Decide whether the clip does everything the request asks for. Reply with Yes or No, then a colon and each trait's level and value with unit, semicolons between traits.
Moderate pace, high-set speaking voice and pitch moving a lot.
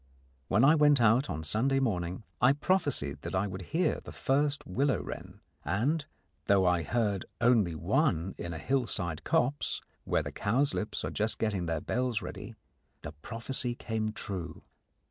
No: average, 165 wpm; low, 110 Hz; wide, 6.7 semitones